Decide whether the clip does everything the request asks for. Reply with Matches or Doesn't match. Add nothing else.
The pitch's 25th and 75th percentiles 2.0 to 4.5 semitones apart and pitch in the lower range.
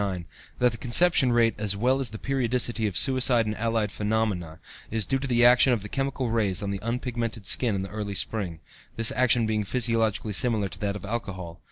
Matches